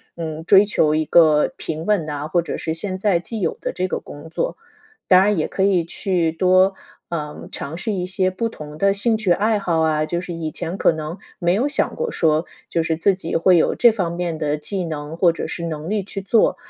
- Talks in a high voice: No, medium, 175 Hz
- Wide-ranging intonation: No, average, 3.5 semitones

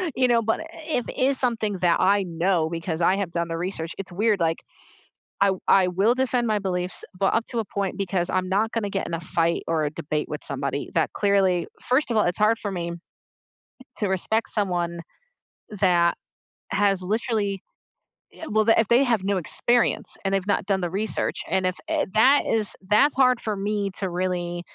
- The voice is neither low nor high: No, high, 195 Hz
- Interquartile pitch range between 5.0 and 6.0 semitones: No, average, 3.8 semitones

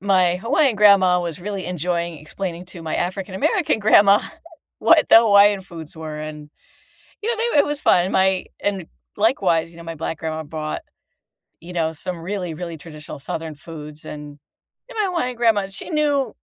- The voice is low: No, medium, 180 Hz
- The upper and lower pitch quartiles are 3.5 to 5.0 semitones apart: Yes, average, 4.2 semitones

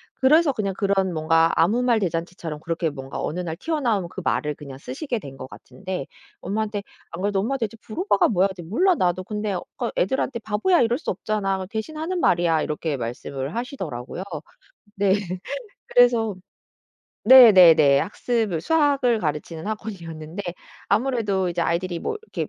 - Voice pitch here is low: No, high, 195 Hz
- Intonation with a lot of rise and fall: Yes, wide, 6.0 semitones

